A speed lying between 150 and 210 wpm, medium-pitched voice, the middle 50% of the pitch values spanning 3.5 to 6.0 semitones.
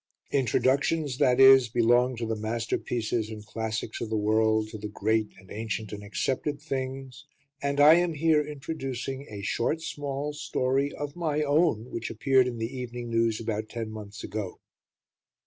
No: average, 165 wpm; low, 120 Hz; average, 4.4 semitones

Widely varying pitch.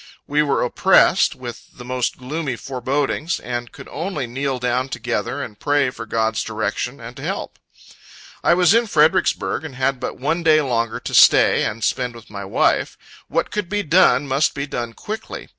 No: average, 3.9 semitones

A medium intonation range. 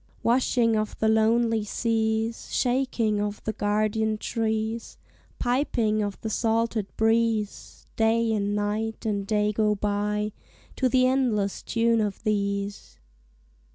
No: narrow, 1.6 semitones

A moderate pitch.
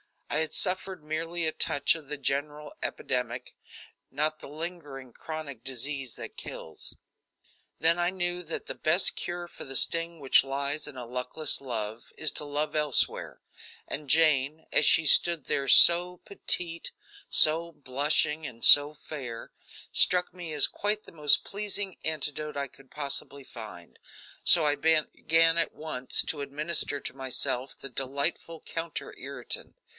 Yes: medium, 150 Hz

